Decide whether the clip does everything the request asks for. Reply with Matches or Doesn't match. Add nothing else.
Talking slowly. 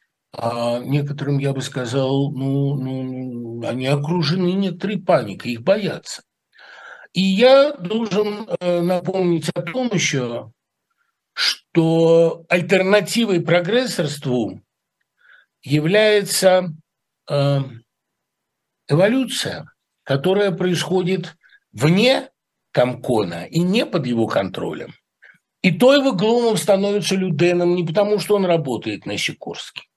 Matches